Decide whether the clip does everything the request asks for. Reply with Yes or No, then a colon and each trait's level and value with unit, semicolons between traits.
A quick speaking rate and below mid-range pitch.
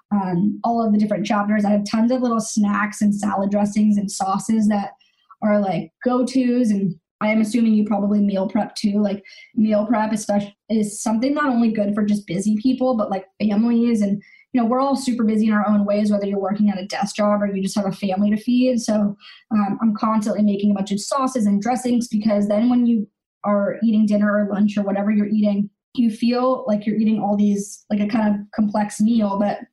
No: fast, 225 wpm; high, 210 Hz